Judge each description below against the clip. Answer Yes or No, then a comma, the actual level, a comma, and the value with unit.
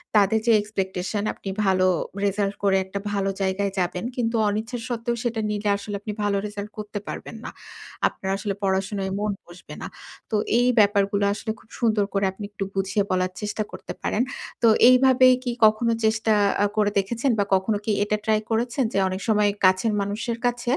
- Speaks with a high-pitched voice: Yes, high, 205 Hz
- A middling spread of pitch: No, narrow, 2.2 semitones